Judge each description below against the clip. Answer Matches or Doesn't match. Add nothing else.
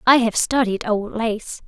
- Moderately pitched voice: Doesn't match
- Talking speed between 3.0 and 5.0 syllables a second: Matches